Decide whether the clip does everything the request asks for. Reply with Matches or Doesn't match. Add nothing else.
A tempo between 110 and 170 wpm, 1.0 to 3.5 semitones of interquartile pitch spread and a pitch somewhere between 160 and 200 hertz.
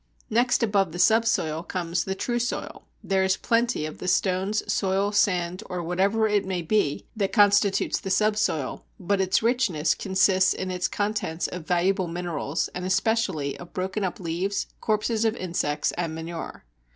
Matches